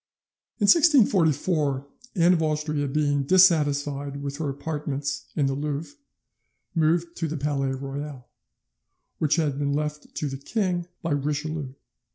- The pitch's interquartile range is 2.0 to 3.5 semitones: Yes, narrow, 2.5 semitones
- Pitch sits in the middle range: Yes, medium, 150 Hz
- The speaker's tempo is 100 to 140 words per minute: Yes, slow, 135 wpm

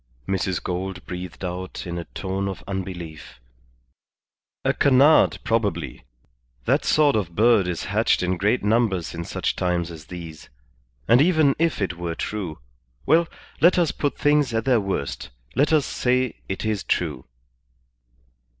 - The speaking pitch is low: Yes, very low, 95 Hz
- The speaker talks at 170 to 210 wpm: No, average, 150 wpm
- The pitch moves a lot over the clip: Yes, wide, 6.3 semitones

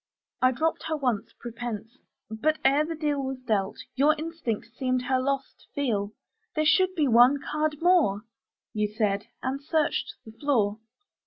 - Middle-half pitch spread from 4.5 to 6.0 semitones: Yes, average, 5.1 semitones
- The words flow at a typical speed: Yes, average, 160 wpm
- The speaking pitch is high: Yes, very high, 265 Hz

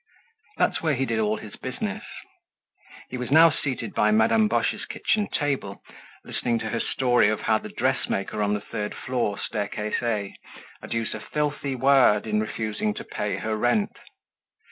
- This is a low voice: Yes, low, 115 Hz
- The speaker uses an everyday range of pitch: Yes, average, 4.3 semitones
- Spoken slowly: No, average, 165 wpm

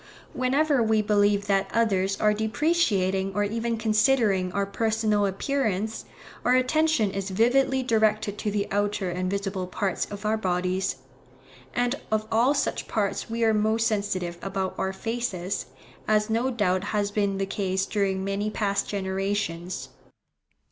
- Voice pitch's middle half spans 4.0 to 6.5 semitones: No, narrow, 2.6 semitones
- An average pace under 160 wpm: Yes, average, 145 wpm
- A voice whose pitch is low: No, high, 205 Hz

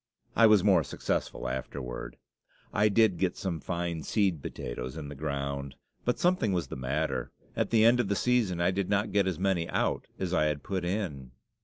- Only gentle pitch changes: No, wide, 5.6 semitones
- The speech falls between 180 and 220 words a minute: Yes, average, 195 wpm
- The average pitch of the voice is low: Yes, very low, 90 Hz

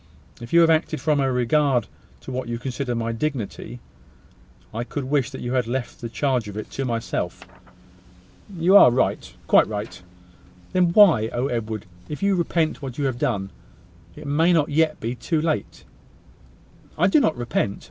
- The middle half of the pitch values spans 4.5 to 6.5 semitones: Yes, average, 4.8 semitones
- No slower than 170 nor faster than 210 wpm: Yes, average, 180 wpm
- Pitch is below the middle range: Yes, low, 130 Hz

